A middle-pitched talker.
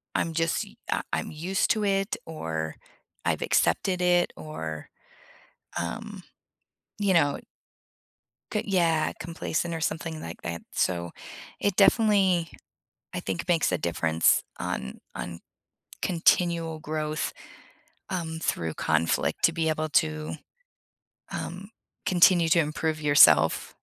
Yes: medium, 160 Hz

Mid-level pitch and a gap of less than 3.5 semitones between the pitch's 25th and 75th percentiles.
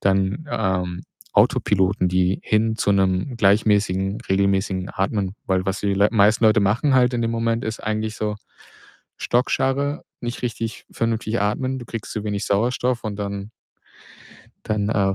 No: low, 105 Hz; average, 2.9 semitones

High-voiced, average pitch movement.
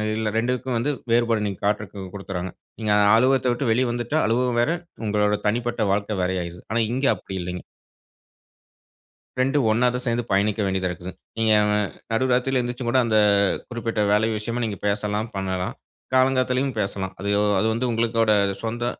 No: low, 115 Hz; average, 3.2 semitones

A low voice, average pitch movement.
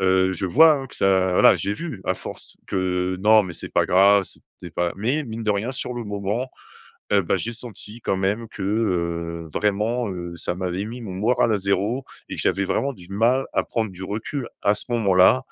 Yes: low, 100 Hz; average, 3.7 semitones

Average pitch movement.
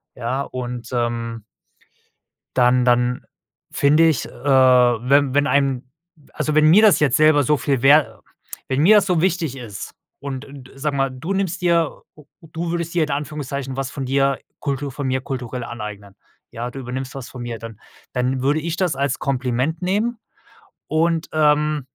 Yes: average, 3.5 semitones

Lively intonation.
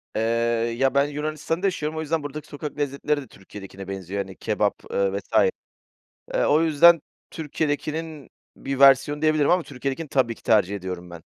Yes: wide, 6.8 semitones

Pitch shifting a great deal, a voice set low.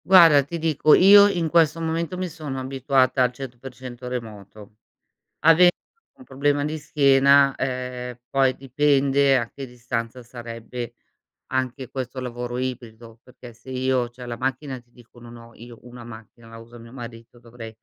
No: average, 2.8 semitones; low, 130 Hz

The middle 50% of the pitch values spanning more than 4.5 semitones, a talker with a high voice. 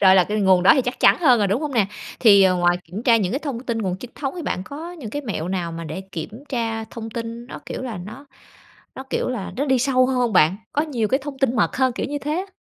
Yes: wide, 5.6 semitones; high, 235 Hz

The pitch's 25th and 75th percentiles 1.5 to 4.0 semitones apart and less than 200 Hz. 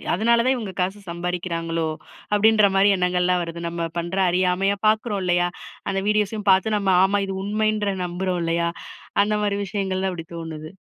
Yes: average, 2.9 semitones; high, 190 Hz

